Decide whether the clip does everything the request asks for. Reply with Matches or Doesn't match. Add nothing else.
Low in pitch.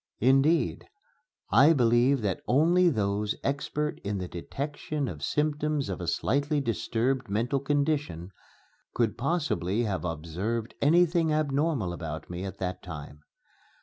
Matches